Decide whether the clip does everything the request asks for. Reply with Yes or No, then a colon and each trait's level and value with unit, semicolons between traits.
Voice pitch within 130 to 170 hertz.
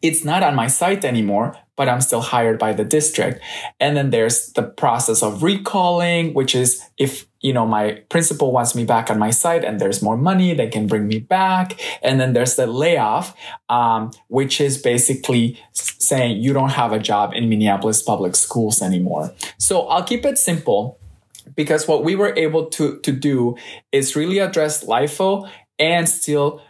Yes: low, 135 Hz